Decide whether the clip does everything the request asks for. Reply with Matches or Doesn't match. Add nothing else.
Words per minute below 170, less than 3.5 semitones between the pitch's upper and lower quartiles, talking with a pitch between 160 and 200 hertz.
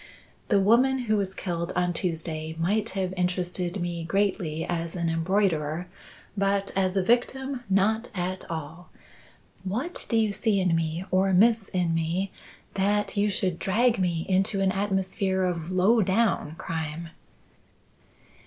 Matches